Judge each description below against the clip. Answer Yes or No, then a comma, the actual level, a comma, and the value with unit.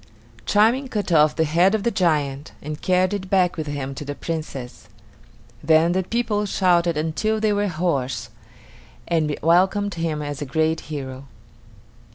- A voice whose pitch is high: No, medium, 165 Hz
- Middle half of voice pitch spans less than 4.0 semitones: No, average, 4.4 semitones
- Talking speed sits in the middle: Yes, average, 160 wpm